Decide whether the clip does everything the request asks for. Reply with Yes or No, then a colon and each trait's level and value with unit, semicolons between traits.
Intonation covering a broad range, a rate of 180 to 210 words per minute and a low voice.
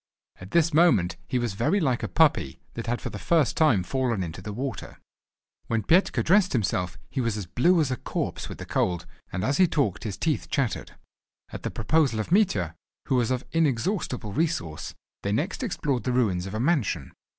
Yes: wide, 7.7 semitones; average, 200 wpm; low, 125 Hz